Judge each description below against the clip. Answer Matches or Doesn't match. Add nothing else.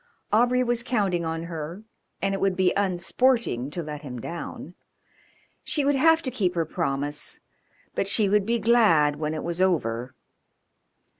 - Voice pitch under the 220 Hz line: Matches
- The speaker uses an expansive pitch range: Matches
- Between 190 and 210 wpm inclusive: Doesn't match